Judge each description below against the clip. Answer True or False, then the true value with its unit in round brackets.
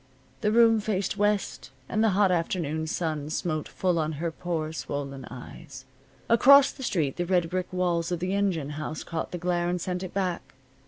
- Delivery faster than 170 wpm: True (190 wpm)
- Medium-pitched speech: True (175 Hz)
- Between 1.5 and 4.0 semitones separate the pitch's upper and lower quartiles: True (3.4 semitones)